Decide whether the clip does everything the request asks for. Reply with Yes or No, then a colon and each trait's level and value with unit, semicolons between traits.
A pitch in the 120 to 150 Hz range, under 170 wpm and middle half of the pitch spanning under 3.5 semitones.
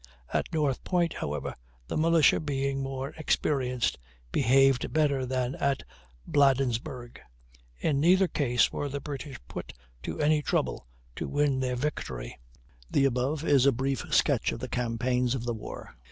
Yes: low, 135 Hz; average, 150 wpm; average, 2.7 semitones